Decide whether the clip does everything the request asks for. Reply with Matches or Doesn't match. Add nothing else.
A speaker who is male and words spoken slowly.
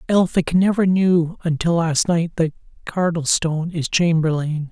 Matches